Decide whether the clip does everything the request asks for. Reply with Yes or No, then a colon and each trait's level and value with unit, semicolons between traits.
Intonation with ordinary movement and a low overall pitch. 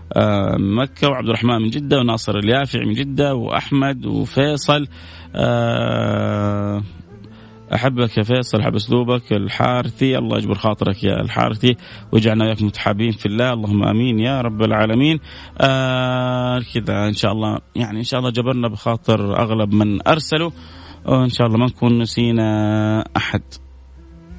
Yes: average, 3.3 semitones; low, 115 Hz